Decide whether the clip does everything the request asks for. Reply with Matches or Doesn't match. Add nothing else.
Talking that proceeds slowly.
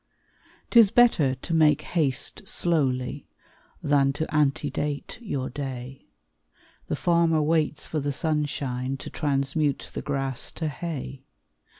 Matches